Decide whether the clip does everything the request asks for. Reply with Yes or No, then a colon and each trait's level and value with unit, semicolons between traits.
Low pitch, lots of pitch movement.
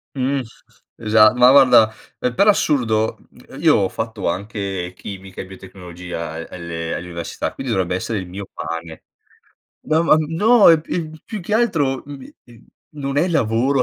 Yes: low, 110 Hz; wide, 7.4 semitones